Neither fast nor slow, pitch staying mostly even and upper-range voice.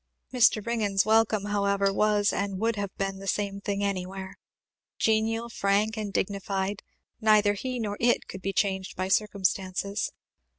Yes: average, 145 wpm; narrow, 1.6 semitones; high, 200 Hz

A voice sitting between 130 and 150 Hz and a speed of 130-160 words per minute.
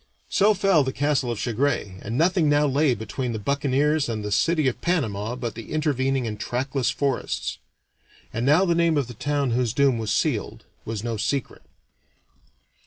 No: low, 135 Hz; average, 175 wpm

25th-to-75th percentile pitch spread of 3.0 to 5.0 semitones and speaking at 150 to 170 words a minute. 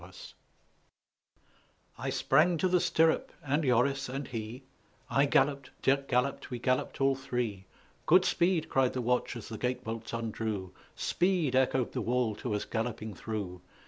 Yes: average, 3.6 semitones; average, 155 wpm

